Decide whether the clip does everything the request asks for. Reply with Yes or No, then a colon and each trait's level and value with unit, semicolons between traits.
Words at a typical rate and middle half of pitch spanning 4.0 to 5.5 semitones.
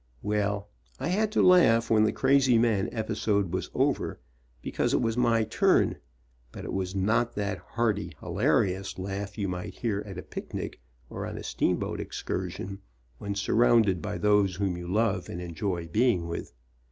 No: average, 170 wpm; average, 3.3 semitones